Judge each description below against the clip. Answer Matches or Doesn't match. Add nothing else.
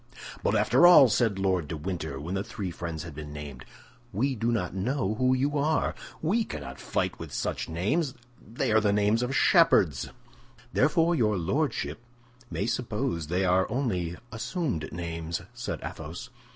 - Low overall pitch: Matches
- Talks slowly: Doesn't match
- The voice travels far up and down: Matches